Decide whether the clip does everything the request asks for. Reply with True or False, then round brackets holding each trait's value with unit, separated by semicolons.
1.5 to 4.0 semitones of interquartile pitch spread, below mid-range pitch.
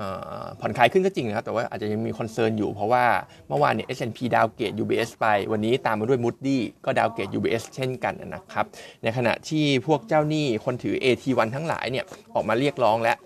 True (3.6 semitones; 125 Hz)